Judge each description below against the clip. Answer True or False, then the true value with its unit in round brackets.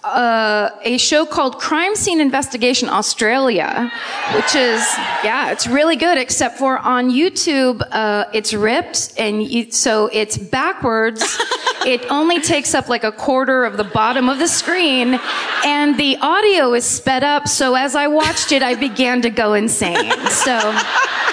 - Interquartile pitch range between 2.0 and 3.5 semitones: False (4.7 semitones)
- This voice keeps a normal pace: True (160 wpm)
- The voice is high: True (265 Hz)